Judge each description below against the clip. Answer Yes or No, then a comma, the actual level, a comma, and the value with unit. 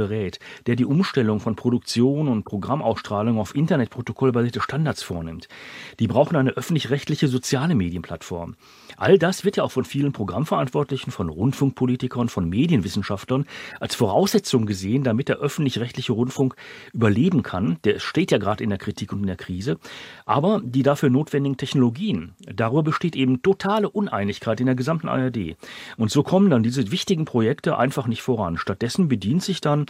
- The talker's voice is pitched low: Yes, low, 130 Hz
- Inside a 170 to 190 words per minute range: No, average, 155 wpm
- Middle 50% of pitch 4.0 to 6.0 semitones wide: Yes, average, 4.5 semitones